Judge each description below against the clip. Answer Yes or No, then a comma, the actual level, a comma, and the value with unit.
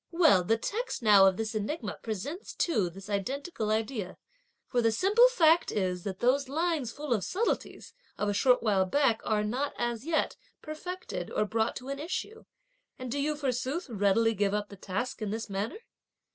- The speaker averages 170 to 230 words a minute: Yes, average, 185 wpm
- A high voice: Yes, high, 235 Hz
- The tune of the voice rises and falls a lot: Yes, wide, 6.2 semitones